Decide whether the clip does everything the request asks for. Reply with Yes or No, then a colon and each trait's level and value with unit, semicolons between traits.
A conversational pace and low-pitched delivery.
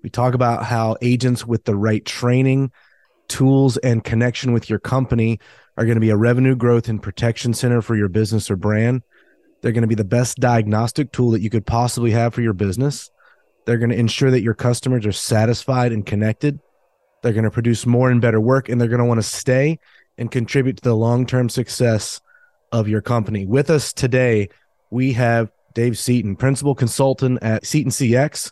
Yes: average, 195 wpm; low, 120 Hz